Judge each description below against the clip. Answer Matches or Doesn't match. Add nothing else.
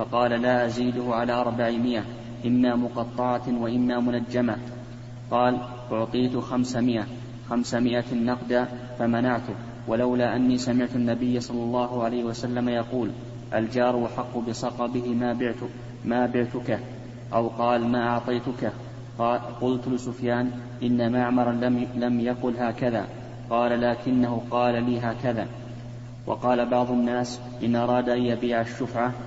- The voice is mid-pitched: Doesn't match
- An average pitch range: Doesn't match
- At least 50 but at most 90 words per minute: Doesn't match